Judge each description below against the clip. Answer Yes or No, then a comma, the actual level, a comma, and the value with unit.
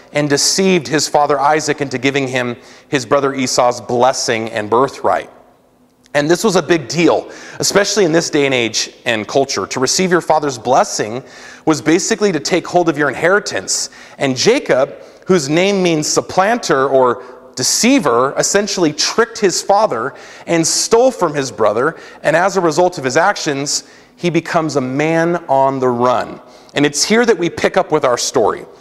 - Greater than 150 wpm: Yes, average, 170 wpm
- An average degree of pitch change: Yes, average, 4.7 semitones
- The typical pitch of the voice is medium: Yes, medium, 155 Hz